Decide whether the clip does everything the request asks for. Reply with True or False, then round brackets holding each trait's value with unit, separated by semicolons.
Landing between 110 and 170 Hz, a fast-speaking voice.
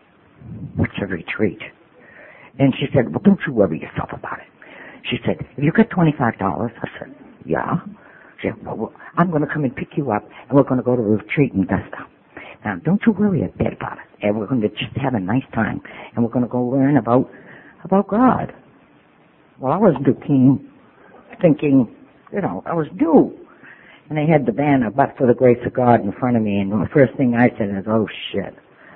True (135 Hz; 220 wpm)